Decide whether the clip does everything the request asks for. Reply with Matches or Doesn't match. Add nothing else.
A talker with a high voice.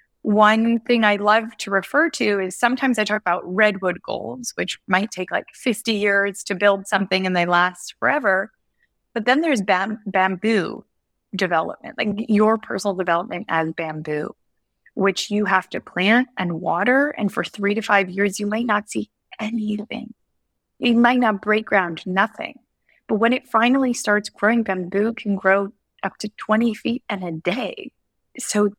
Matches